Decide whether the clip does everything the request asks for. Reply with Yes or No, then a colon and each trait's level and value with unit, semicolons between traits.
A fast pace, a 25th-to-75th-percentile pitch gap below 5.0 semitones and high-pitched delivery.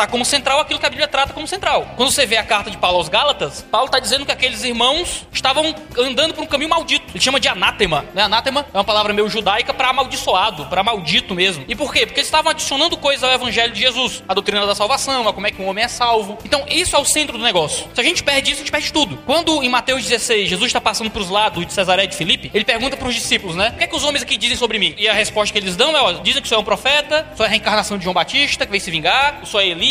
No: fast, 285 wpm; wide, 5.4 semitones; high, 245 Hz